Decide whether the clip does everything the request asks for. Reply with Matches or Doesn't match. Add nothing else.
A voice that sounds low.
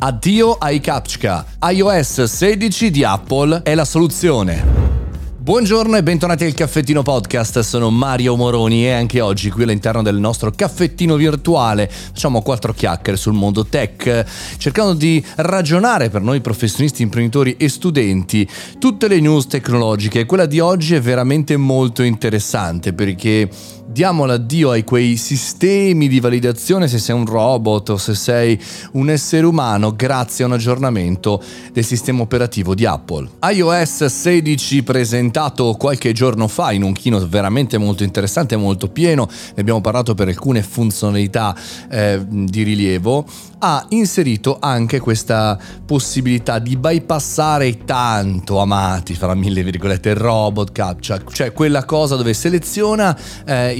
Matches